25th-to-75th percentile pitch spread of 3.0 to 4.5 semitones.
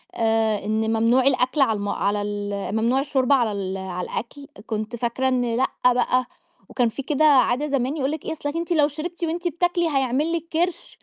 No: average, 5.2 semitones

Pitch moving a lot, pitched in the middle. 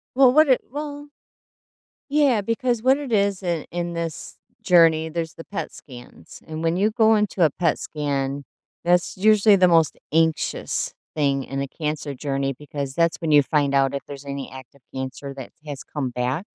Yes: wide, 6.4 semitones; medium, 160 Hz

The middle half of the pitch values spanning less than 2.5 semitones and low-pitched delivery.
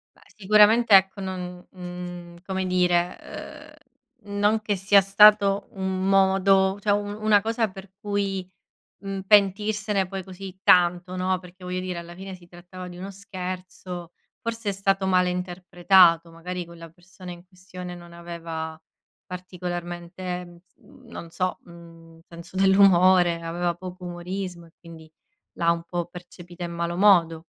No: narrow, 1.9 semitones; medium, 185 Hz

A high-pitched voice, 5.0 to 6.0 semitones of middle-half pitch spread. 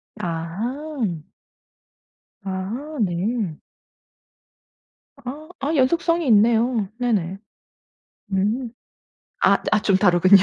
Yes: high, 220 Hz; wide, 5.6 semitones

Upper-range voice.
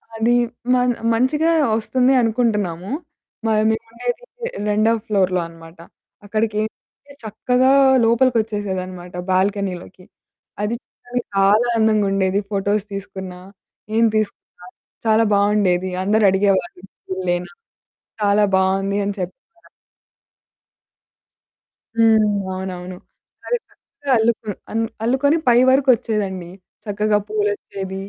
Yes: high, 210 Hz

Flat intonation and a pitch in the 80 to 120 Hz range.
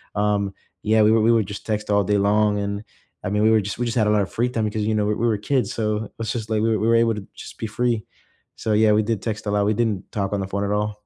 Yes: narrow, 1.4 semitones; low, 105 Hz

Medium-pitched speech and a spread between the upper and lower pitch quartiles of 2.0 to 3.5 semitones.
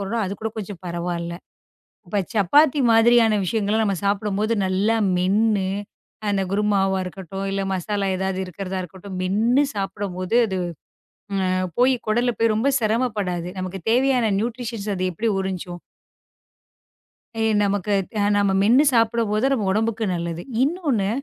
No: high, 205 Hz; average, 3.1 semitones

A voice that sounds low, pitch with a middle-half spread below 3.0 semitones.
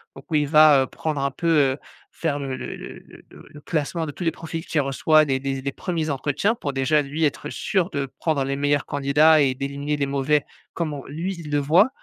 No: medium, 145 Hz; narrow, 2.4 semitones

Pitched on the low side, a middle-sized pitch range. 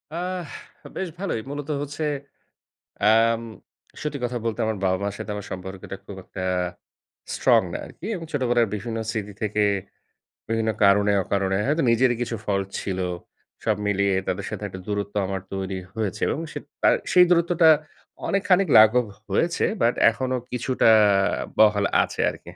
No: low, 115 Hz; wide, 6.1 semitones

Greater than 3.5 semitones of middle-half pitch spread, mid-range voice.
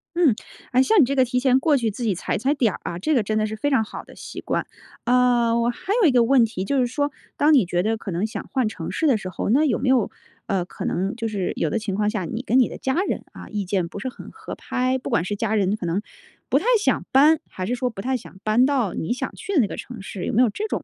No: average, 4.3 semitones; high, 235 Hz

